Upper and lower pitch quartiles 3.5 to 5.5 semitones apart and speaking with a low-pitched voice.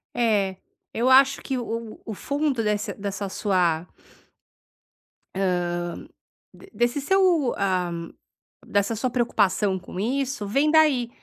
No: average, 5.2 semitones; high, 225 Hz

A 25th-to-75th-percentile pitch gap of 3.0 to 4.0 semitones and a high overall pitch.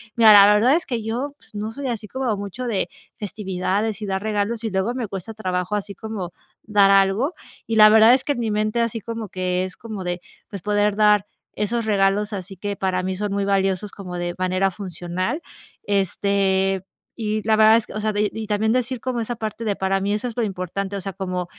No: narrow, 2.5 semitones; high, 205 Hz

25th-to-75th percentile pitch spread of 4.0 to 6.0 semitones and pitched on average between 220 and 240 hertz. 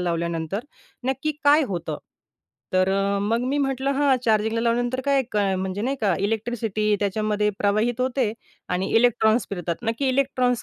Yes: average, 4.3 semitones; high, 225 Hz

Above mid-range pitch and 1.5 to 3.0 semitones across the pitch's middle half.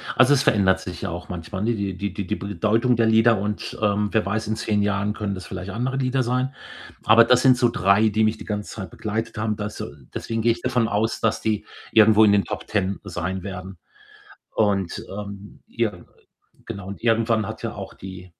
No: low, 105 Hz; narrow, 2.4 semitones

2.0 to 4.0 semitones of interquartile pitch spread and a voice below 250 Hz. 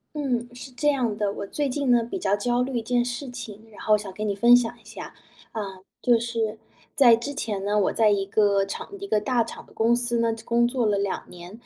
Yes: average, 2.9 semitones; high, 230 Hz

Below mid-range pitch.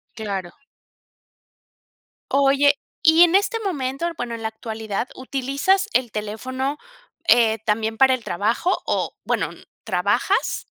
No: very high, 255 Hz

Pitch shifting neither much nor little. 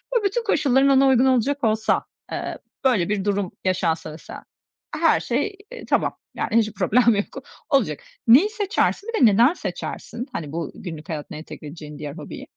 No: wide, 8.3 semitones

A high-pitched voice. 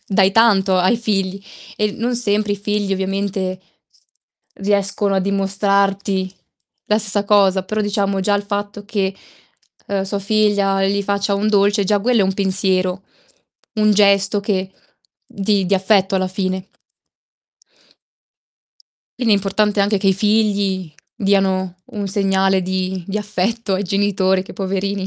Yes: high, 200 Hz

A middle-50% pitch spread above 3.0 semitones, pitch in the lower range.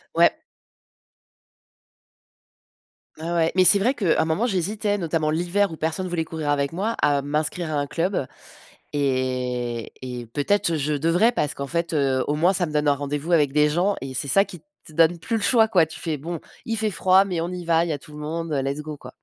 No: average, 3.8 semitones; medium, 160 Hz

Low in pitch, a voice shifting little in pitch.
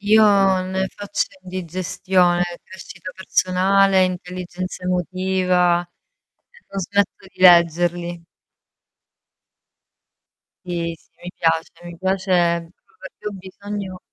No: medium, 185 Hz; narrow, 1.5 semitones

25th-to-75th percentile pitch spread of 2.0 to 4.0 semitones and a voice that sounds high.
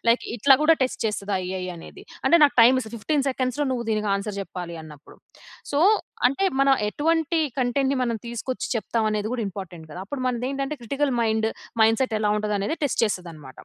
No: average, 4.7 semitones; high, 230 Hz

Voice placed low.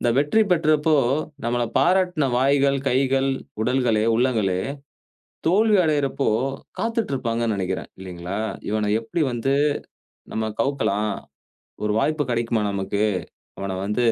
Yes: low, 125 Hz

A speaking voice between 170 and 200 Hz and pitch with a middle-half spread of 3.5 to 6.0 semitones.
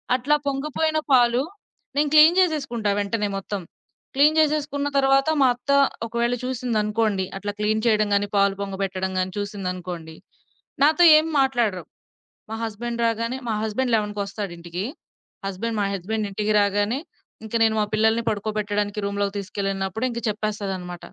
No: high, 215 Hz; average, 3.8 semitones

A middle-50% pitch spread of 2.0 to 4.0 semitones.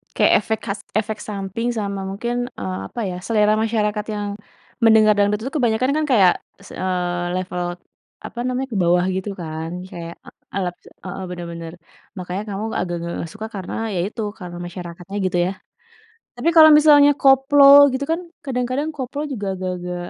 No: average, 4.9 semitones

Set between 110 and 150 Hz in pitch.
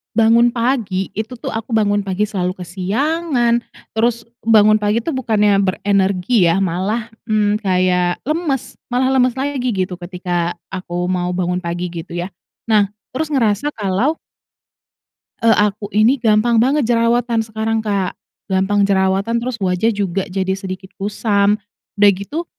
No: high, 210 Hz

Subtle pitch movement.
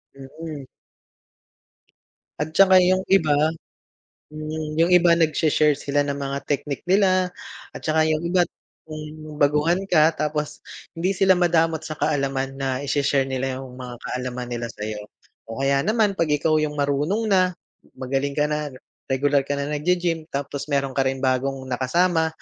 No: average, 3.5 semitones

